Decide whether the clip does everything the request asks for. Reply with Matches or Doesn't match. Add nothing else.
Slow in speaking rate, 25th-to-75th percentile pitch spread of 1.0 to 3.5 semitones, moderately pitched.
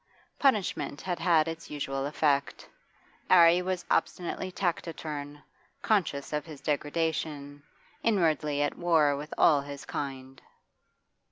Matches